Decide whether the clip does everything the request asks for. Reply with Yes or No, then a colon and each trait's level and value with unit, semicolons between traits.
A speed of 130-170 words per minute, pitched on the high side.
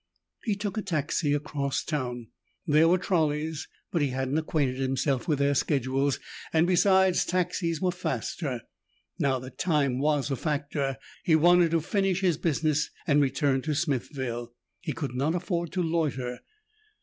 No: average, 155 wpm; medium, 150 Hz